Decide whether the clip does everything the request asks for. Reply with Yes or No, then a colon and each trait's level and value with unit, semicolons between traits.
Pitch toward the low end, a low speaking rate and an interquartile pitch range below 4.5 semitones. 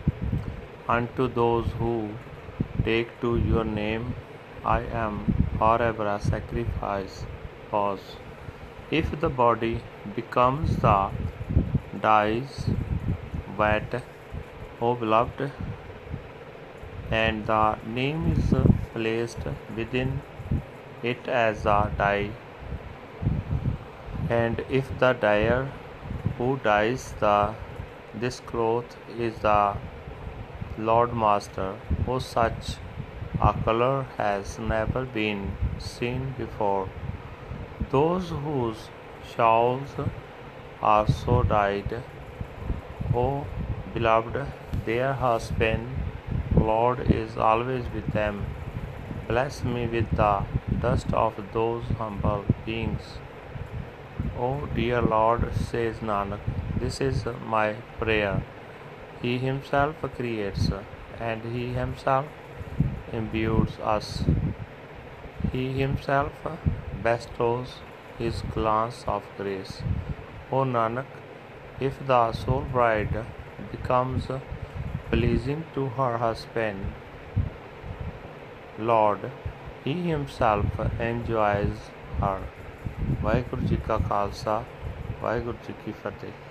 Yes: low, 115 Hz; slow, 85 wpm; average, 2.8 semitones